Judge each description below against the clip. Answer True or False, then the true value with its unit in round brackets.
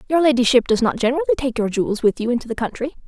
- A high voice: True (255 Hz)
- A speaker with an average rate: False (255 wpm)